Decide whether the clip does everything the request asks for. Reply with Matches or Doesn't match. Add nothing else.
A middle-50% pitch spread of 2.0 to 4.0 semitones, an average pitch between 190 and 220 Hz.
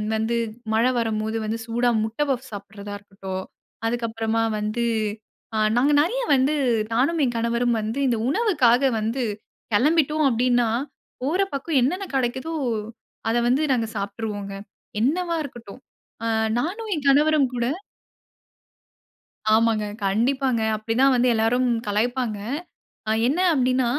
Doesn't match